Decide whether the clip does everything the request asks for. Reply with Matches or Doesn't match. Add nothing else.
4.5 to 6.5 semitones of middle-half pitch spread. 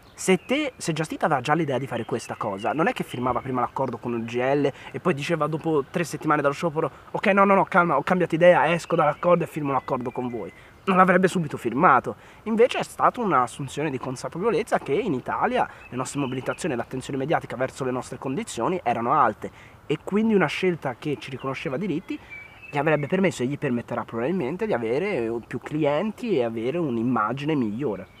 Matches